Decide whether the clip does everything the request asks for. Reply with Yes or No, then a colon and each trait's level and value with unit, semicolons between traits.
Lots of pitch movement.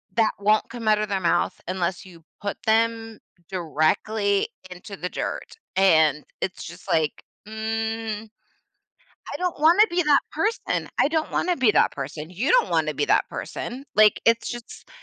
No: average, 4.4 semitones